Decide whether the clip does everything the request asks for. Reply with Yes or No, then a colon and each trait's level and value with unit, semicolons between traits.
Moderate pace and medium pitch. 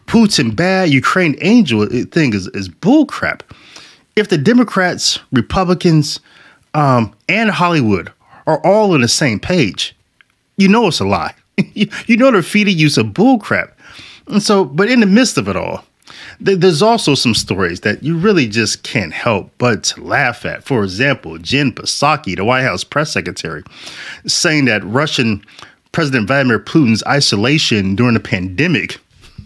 Yes: average, 155 wpm; medium, 150 Hz